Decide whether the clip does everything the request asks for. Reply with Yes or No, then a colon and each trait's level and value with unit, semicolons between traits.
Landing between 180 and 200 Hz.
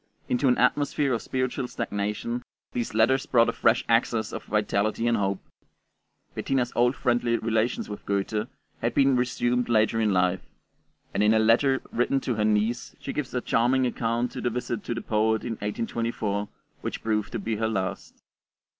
No: low, 115 Hz